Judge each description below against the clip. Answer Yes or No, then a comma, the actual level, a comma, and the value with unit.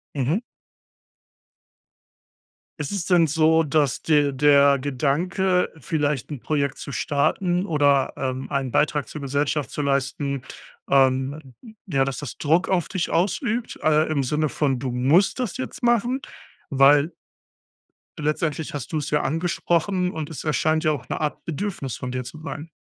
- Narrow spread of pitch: No, average, 3.2 semitones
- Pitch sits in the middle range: Yes, medium, 150 Hz